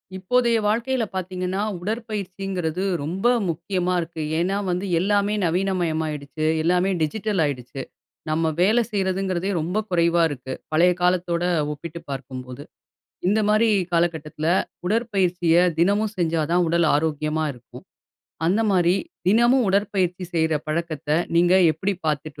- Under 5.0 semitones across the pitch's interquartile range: Yes, average, 3.4 semitones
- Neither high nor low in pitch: Yes, medium, 180 Hz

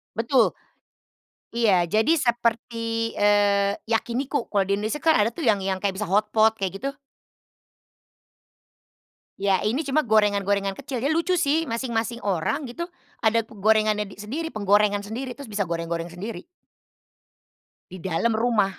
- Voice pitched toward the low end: No, high, 220 Hz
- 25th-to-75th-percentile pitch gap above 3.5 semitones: No, average, 3.2 semitones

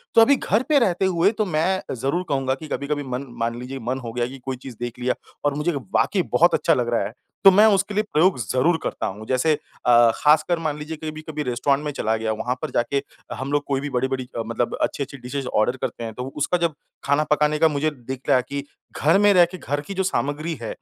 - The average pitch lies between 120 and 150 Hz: Yes, medium, 140 Hz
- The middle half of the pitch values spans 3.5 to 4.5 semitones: Yes, average, 4.2 semitones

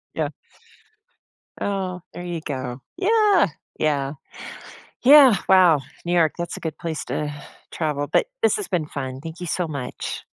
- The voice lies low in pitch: No, medium, 165 Hz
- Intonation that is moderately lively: Yes, average, 4.2 semitones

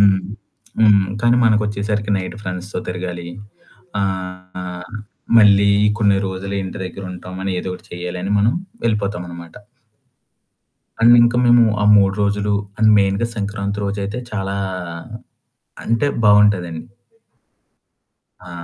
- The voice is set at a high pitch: No, low, 100 Hz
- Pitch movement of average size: No, narrow, 2.2 semitones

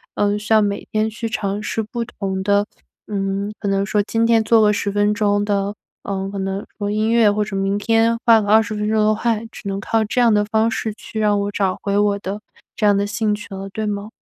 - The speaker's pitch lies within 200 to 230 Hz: Yes, high, 210 Hz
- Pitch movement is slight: Yes, narrow, 1.5 semitones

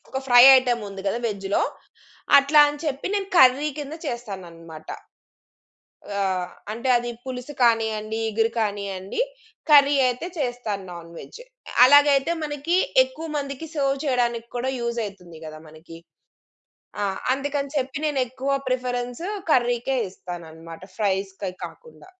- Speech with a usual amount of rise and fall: No, wide, 5.7 semitones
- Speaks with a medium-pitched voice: No, high, 245 Hz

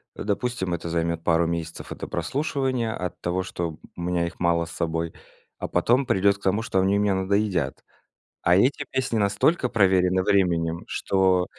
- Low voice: Yes, very low, 95 Hz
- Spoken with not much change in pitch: No, average, 3.4 semitones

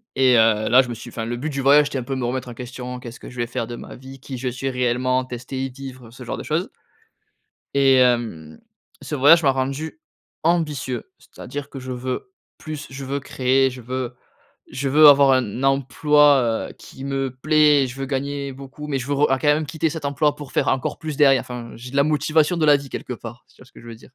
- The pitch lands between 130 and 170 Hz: Yes, low, 135 Hz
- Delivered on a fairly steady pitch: Yes, narrow, 2.3 semitones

